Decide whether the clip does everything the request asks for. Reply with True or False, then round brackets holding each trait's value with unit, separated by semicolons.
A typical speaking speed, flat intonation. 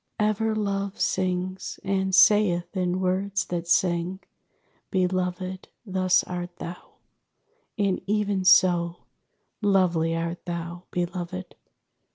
False (105 wpm; 1.7 semitones)